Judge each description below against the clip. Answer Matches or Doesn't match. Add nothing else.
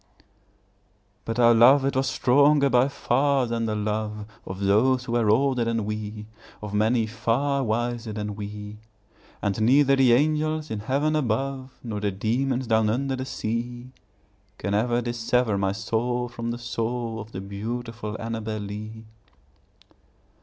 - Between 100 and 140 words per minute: Doesn't match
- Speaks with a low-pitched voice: Matches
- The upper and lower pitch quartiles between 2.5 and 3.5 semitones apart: Matches